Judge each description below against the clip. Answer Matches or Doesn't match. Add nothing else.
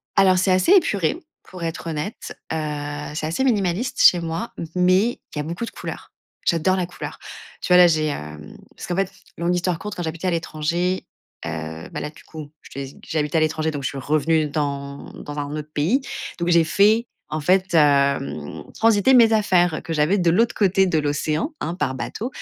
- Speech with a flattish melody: Doesn't match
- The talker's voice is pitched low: Doesn't match